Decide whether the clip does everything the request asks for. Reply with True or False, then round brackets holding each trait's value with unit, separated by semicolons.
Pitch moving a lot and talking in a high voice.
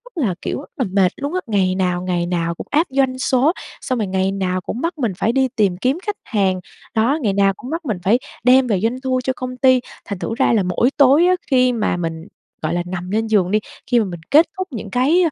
True (5.9 semitones; 225 Hz)